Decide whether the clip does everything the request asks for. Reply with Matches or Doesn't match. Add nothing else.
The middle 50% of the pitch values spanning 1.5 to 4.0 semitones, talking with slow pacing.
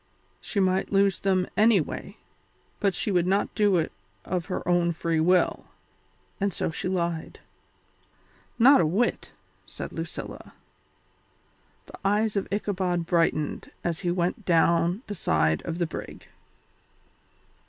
Matches